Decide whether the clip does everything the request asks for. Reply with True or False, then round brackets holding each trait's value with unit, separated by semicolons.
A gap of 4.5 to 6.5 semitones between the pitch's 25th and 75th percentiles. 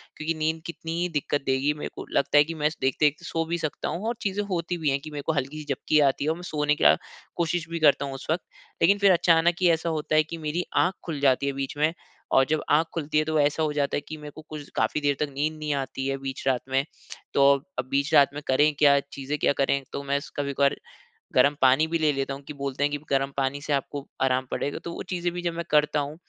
False (2.5 semitones)